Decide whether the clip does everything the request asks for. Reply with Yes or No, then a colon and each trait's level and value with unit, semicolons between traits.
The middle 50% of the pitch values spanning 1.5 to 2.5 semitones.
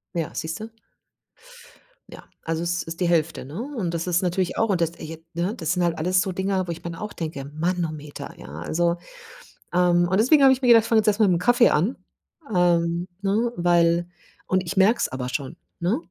No: average, 2.9 semitones